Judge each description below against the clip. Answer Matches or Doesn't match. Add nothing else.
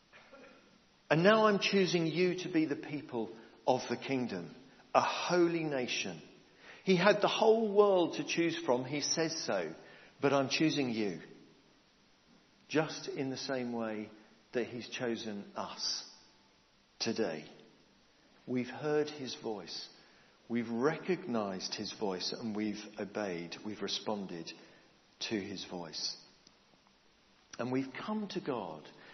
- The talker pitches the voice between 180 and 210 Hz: Doesn't match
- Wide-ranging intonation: Matches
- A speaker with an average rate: Doesn't match